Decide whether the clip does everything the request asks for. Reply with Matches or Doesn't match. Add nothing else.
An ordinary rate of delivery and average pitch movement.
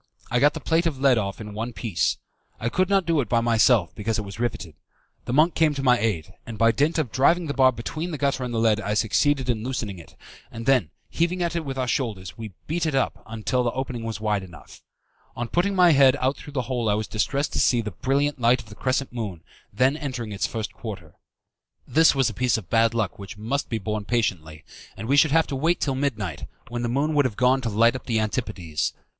Doesn't match